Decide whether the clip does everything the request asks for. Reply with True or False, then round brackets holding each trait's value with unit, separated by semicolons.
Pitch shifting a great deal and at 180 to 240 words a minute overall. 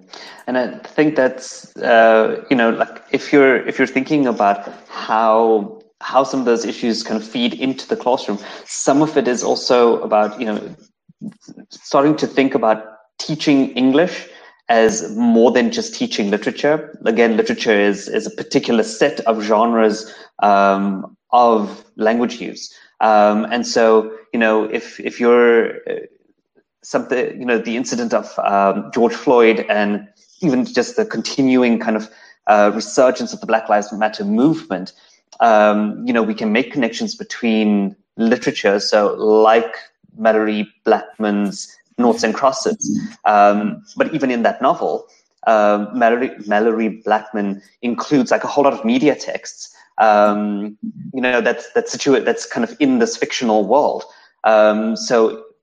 False (6.2 semitones; 150 wpm)